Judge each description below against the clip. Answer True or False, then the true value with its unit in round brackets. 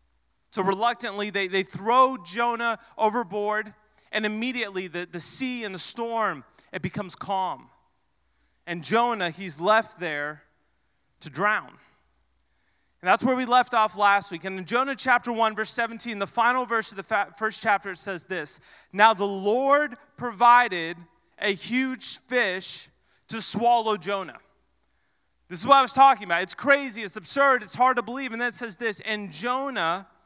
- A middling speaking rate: True (165 wpm)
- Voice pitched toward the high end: True (215 Hz)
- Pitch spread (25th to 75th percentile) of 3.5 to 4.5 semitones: False (4.9 semitones)